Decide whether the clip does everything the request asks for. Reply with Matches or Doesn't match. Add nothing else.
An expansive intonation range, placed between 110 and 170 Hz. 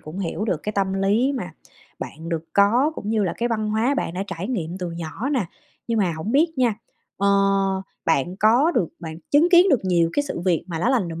Doesn't match